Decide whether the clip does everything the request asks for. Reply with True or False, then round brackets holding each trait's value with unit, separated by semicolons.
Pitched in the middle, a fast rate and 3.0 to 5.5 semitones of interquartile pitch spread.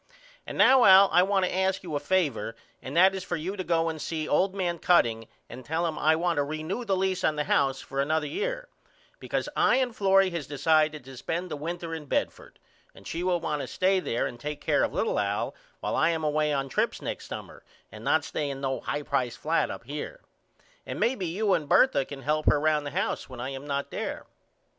True (160 Hz; 235 wpm; 4.5 semitones)